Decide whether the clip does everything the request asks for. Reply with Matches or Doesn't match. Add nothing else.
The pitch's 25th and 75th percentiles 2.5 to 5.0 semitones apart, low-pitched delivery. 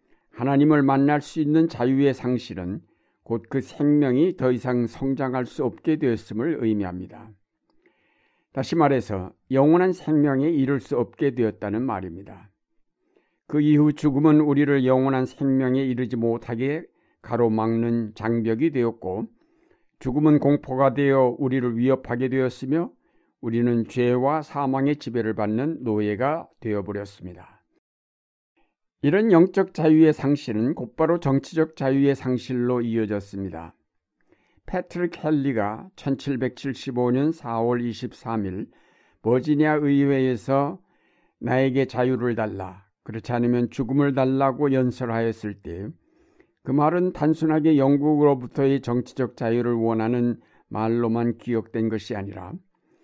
Matches